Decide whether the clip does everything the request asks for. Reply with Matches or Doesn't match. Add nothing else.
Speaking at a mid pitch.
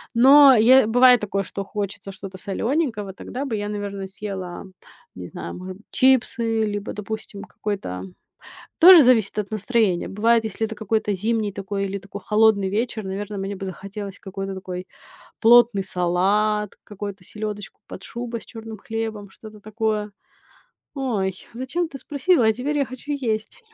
Doesn't match